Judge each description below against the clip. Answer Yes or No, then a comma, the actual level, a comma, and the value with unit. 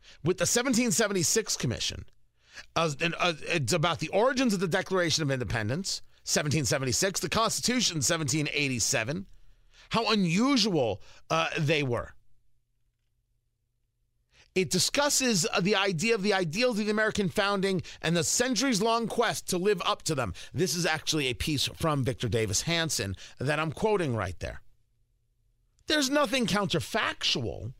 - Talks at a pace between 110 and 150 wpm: Yes, average, 140 wpm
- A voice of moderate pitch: Yes, medium, 165 Hz